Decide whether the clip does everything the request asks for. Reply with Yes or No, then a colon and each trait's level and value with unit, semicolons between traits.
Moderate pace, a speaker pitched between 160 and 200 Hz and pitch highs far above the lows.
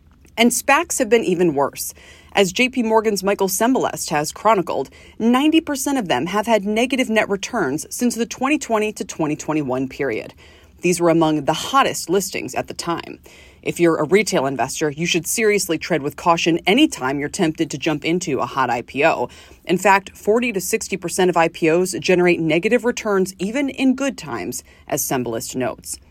Yes: average, 170 wpm; medium, 185 Hz; wide, 6.3 semitones